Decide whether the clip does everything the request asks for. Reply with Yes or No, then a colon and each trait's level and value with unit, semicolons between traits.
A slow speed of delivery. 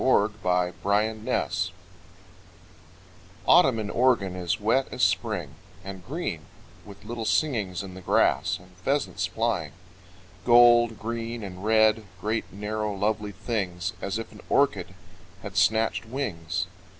Yes: slow, 125 wpm